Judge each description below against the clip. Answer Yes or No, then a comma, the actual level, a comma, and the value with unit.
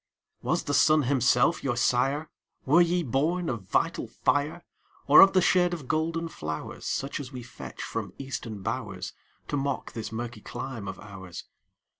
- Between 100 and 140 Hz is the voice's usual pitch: Yes, low, 135 Hz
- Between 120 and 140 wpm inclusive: No, average, 165 wpm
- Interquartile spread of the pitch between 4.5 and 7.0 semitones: Yes, average, 4.9 semitones